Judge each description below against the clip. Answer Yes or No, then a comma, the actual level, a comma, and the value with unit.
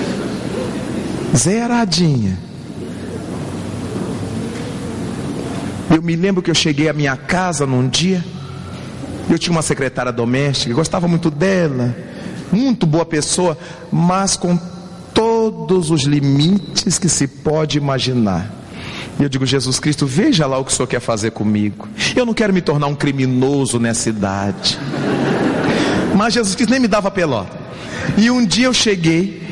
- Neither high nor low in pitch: Yes, medium, 160 Hz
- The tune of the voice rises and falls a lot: Yes, wide, 5.7 semitones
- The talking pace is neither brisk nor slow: Yes, average, 140 wpm